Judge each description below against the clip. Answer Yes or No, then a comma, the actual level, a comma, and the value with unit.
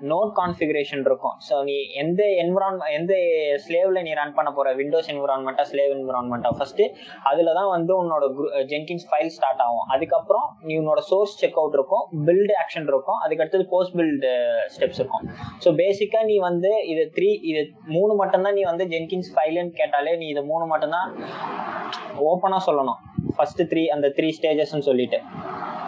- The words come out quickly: Yes, fast, 160 wpm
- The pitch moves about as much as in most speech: Yes, average, 4.8 semitones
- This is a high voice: No, medium, 170 Hz